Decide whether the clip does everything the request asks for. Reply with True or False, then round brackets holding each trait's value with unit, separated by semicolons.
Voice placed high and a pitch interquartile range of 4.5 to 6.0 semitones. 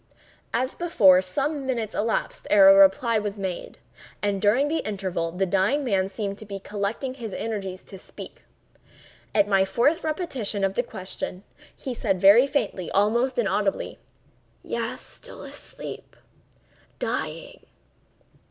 True (205 Hz; 4.8 semitones)